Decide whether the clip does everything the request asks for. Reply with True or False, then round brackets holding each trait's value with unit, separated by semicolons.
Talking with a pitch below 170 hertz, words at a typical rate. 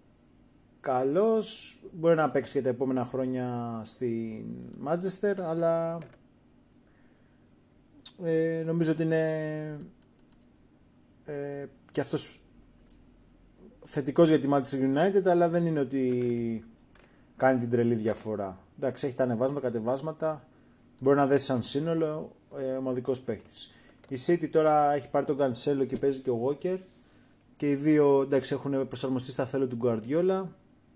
True (140 Hz; 130 wpm)